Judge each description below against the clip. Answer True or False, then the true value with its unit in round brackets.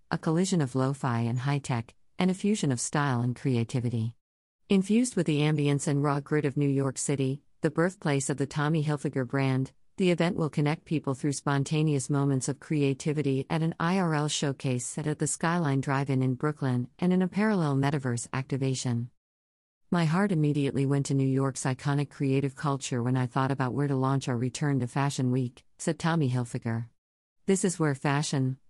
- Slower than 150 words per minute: False (190 wpm)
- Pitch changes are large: False (2.8 semitones)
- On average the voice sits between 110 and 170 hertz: True (140 Hz)